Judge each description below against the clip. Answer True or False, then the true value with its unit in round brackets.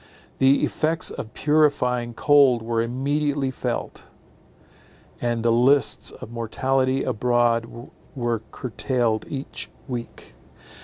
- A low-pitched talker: True (125 Hz)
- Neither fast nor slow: False (100 wpm)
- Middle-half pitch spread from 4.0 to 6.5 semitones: False (2.6 semitones)